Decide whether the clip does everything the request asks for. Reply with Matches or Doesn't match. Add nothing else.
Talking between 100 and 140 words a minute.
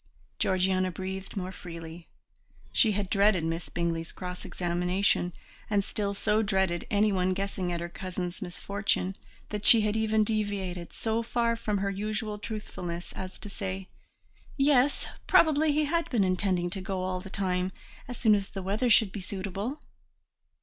Doesn't match